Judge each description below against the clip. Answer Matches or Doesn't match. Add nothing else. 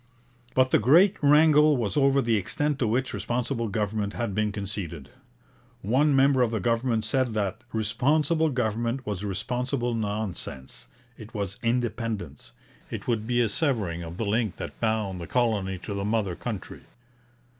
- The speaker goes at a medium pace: Matches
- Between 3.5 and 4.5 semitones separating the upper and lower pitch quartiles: Matches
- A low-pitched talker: Matches